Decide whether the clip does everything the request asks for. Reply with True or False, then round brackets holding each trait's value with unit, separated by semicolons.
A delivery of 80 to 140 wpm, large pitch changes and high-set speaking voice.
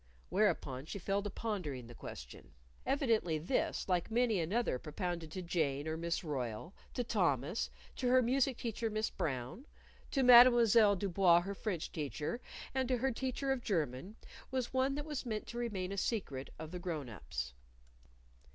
False (170 wpm; 7.4 semitones; 195 Hz)